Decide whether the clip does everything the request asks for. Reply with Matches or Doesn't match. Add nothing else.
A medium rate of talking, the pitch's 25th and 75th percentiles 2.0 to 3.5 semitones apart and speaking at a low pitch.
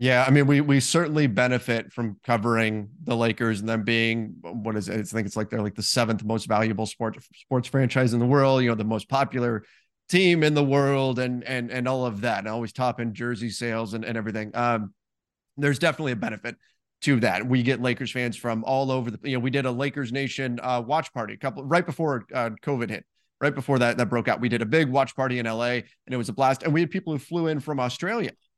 Doesn't match